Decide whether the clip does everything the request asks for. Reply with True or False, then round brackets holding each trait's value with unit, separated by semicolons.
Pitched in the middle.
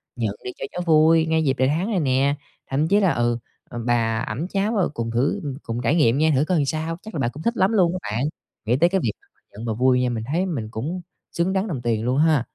True (145 Hz)